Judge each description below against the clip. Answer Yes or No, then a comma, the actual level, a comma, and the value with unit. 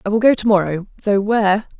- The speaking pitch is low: No, high, 205 Hz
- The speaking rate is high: Yes, fast, 235 wpm